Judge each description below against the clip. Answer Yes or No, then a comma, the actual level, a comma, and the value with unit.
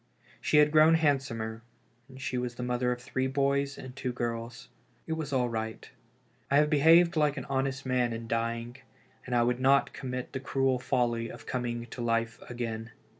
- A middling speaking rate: Yes, average, 185 wpm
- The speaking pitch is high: No, low, 125 Hz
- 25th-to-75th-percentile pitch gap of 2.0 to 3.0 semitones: Yes, average, 2.7 semitones